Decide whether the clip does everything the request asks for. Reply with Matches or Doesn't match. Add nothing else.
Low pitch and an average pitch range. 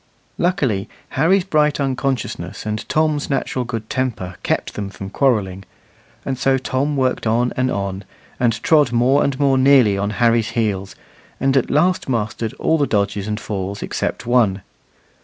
Matches